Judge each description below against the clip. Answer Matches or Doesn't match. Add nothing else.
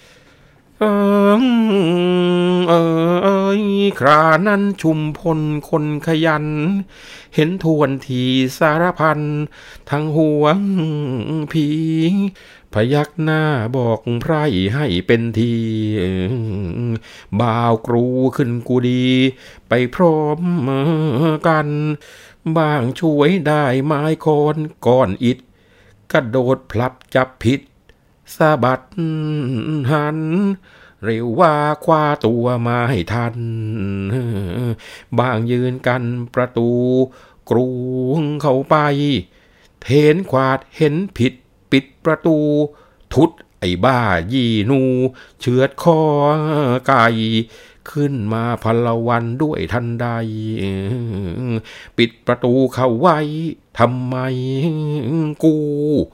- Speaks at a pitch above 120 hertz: Matches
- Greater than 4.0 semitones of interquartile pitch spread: Matches